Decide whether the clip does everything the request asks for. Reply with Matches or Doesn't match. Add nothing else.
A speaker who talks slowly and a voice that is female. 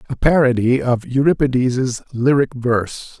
Doesn't match